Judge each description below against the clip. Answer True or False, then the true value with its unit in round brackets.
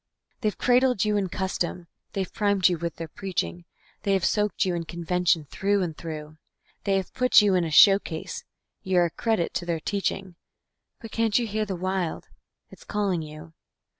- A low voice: False (185 Hz)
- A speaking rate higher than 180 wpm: True (190 wpm)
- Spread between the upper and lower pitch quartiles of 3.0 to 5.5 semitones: True (3.3 semitones)